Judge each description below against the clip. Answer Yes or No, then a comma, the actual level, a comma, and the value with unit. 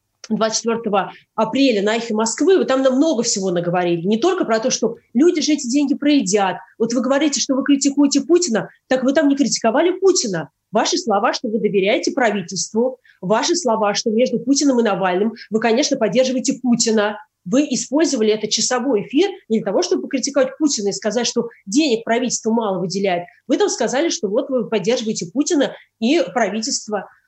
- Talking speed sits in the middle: No, fast, 175 wpm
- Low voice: No, high, 235 Hz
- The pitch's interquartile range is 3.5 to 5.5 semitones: Yes, average, 4.6 semitones